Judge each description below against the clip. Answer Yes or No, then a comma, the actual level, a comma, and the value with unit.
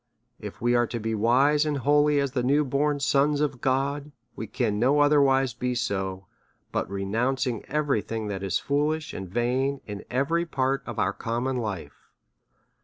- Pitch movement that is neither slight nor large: Yes, average, 4.2 semitones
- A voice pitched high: No, low, 130 Hz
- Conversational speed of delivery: Yes, average, 180 wpm